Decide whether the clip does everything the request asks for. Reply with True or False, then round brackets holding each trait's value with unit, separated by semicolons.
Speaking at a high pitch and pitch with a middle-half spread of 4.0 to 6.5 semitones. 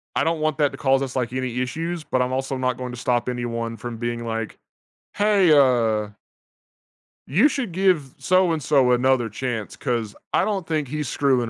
False (130 Hz; 4.3 semitones)